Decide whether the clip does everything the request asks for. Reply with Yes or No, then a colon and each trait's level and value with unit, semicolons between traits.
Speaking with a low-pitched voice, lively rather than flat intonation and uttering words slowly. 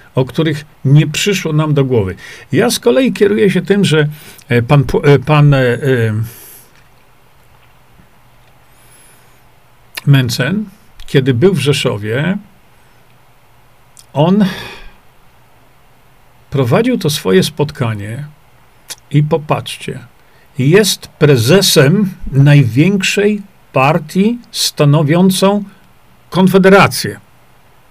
No: medium, 150 Hz; wide, 6.5 semitones; slow, 75 wpm